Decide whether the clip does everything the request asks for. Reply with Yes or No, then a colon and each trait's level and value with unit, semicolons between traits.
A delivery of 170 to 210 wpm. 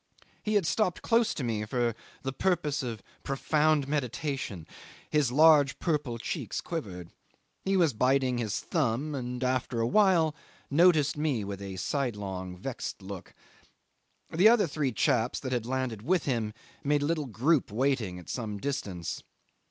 No: average, 150 wpm